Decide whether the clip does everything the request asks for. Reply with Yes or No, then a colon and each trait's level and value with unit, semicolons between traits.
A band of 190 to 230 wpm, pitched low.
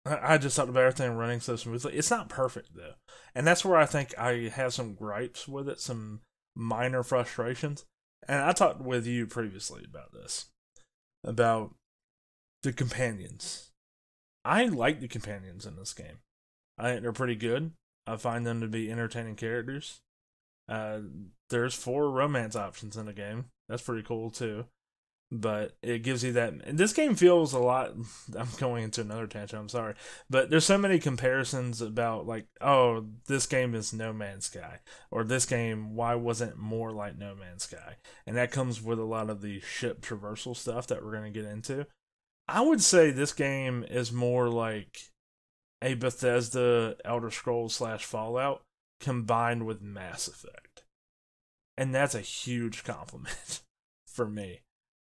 No: average, 165 wpm; low, 120 Hz